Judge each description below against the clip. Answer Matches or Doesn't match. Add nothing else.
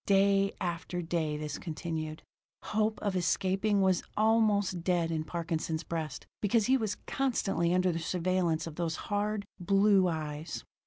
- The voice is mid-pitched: Matches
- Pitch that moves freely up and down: Doesn't match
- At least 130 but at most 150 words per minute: Matches